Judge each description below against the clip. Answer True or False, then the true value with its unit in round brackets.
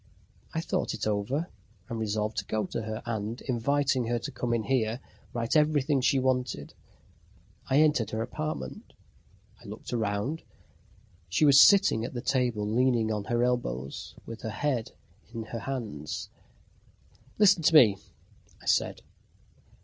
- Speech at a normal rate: True (150 wpm)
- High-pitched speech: False (120 Hz)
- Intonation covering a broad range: False (3.7 semitones)